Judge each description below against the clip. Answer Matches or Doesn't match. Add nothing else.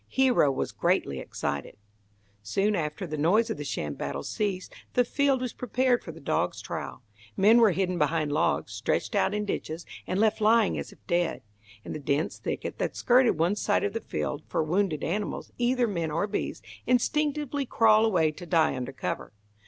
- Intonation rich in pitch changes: Matches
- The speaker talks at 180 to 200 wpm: Matches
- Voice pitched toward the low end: Doesn't match